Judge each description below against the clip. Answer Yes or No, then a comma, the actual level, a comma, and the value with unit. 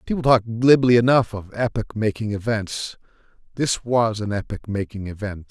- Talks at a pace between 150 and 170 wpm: Yes, average, 155 wpm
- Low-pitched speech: Yes, low, 110 Hz